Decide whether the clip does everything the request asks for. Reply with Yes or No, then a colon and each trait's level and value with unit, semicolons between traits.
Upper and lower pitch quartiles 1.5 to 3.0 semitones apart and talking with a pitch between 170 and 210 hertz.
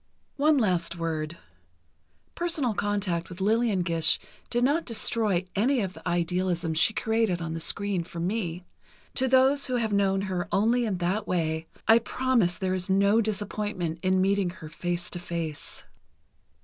No: average, 4.4 semitones; high, 190 Hz